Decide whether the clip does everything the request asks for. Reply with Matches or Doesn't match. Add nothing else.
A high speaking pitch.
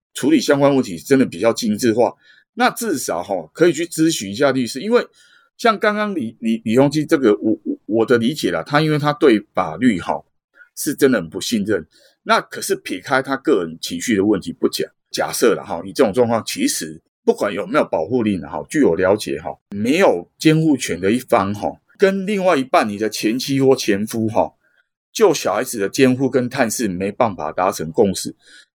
Doesn't match